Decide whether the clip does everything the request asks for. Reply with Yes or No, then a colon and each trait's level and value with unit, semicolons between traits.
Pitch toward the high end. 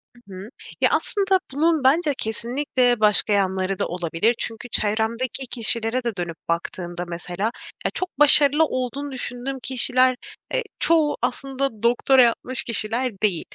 Yes: high, 245 Hz